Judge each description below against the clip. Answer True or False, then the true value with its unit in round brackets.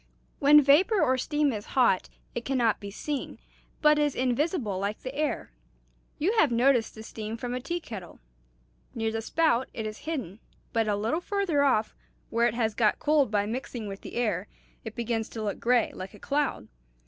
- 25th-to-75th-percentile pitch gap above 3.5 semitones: True (5.1 semitones)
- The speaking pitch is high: True (240 Hz)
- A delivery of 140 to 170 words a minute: False (195 wpm)